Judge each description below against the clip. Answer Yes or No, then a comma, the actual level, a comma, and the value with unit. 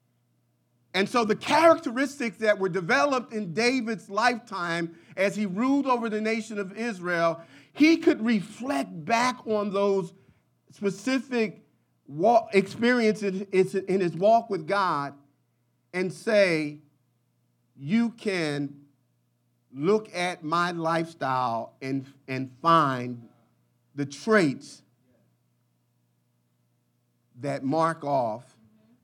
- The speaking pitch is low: No, medium, 170 Hz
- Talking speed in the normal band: No, slow, 95 wpm